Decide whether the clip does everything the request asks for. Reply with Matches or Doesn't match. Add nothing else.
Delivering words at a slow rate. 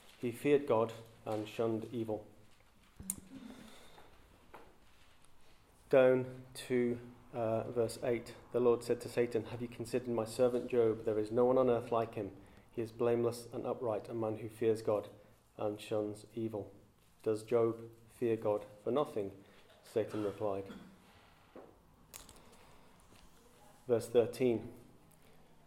Matches